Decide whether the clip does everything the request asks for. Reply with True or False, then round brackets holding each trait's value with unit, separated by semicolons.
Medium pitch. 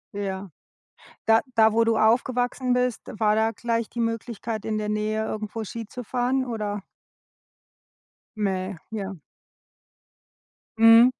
False (225 Hz)